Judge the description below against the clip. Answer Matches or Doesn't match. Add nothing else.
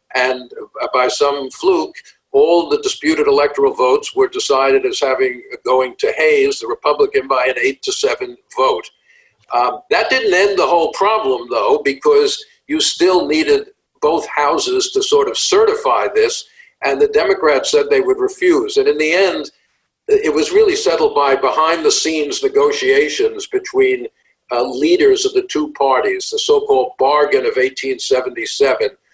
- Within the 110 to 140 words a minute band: Doesn't match